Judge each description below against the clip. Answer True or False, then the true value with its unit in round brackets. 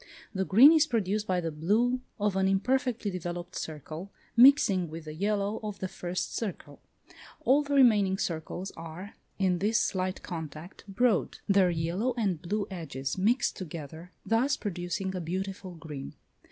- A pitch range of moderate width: True (3.8 semitones)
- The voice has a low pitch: False (190 Hz)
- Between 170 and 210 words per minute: False (155 wpm)